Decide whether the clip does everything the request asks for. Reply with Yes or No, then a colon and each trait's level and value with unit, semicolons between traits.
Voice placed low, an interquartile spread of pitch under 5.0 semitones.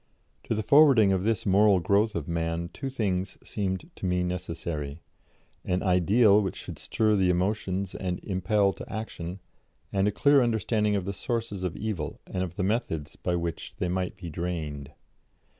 Yes: very low, 95 Hz; average, 3.3 semitones